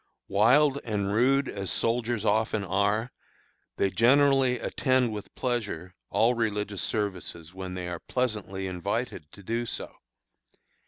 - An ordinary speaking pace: No, slow, 125 wpm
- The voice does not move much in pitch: No, average, 4.0 semitones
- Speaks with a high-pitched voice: No, low, 105 Hz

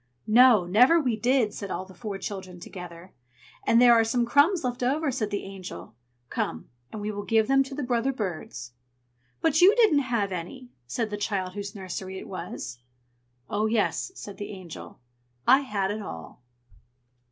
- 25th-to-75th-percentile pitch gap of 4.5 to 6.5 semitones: Yes, average, 5.0 semitones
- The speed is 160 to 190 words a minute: Yes, average, 175 wpm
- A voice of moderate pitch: No, high, 215 Hz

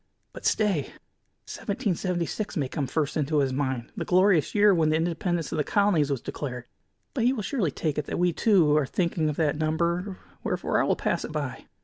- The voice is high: No, medium, 165 Hz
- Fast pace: Yes, fast, 215 wpm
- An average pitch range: Yes, average, 4.0 semitones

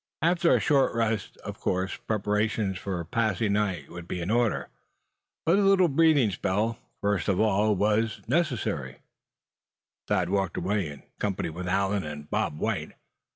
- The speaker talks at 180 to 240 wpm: No, average, 160 wpm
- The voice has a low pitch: Yes, low, 105 Hz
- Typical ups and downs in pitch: Yes, average, 3.7 semitones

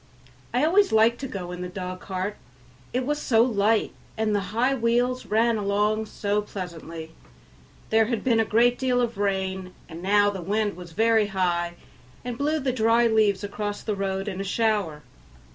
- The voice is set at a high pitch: Yes, high, 210 Hz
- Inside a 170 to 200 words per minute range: Yes, average, 180 wpm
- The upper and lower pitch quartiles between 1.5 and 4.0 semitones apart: Yes, average, 3.3 semitones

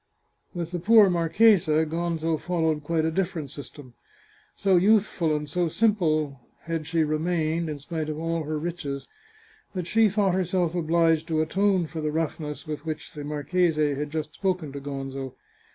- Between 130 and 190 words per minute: Yes, average, 170 wpm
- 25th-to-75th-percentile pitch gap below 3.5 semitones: Yes, average, 2.7 semitones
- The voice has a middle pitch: Yes, medium, 160 Hz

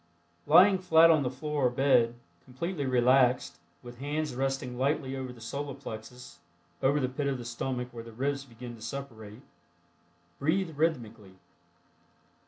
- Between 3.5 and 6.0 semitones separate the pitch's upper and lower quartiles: No, average, 3.1 semitones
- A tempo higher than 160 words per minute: No, average, 150 wpm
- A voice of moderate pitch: No, low, 130 Hz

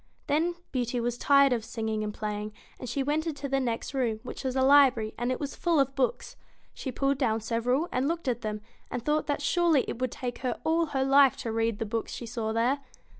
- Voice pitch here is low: No, very high, 255 Hz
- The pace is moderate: No, fast, 230 wpm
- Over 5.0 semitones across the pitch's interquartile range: No, average, 3.6 semitones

